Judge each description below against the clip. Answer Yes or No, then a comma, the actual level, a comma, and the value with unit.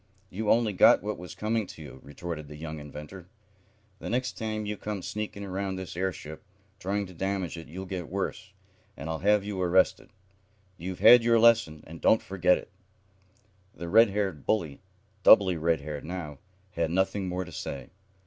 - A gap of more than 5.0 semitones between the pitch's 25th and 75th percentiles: No, average, 4.0 semitones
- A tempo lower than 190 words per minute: Yes, average, 175 wpm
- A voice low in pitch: Yes, very low, 95 Hz